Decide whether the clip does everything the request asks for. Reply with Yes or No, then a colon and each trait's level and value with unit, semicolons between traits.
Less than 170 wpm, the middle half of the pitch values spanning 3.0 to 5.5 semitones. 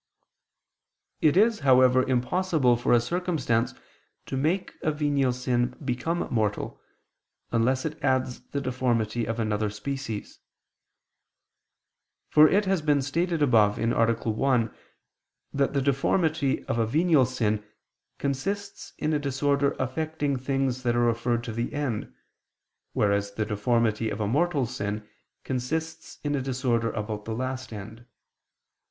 Yes: slow, 135 wpm; average, 3.9 semitones